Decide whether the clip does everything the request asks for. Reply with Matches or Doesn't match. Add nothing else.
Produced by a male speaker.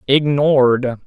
Matches